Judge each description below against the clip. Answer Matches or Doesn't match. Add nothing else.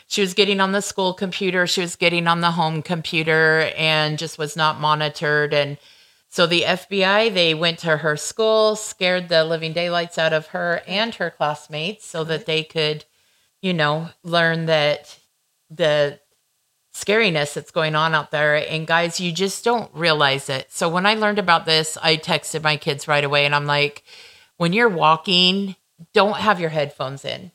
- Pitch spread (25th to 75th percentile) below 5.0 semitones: Matches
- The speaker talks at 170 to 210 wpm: Matches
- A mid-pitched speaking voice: Matches